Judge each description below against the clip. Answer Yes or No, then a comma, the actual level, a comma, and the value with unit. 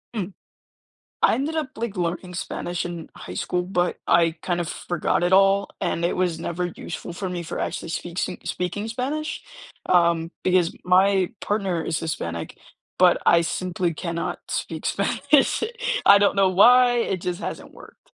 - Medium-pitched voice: Yes, medium, 180 Hz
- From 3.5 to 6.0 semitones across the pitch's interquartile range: No, average, 2.7 semitones